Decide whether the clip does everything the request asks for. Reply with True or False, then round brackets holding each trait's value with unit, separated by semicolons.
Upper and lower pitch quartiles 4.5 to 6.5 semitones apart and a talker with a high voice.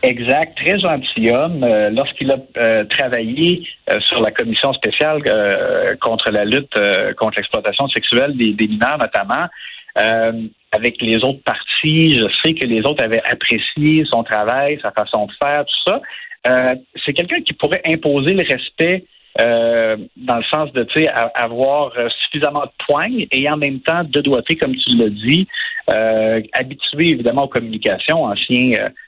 False (5.5 semitones; 140 Hz)